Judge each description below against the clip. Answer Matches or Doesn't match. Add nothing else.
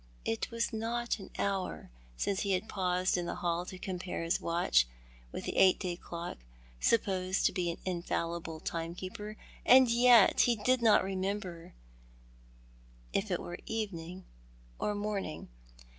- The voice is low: Doesn't match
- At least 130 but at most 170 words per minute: Matches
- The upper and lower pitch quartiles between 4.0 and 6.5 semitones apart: Doesn't match